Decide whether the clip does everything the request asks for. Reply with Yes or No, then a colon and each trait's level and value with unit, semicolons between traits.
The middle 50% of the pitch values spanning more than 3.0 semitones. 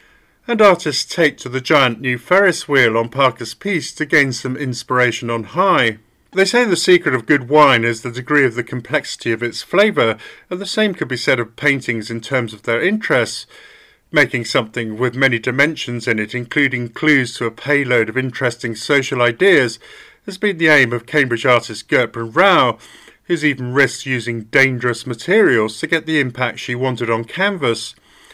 Yes: average, 4.6 semitones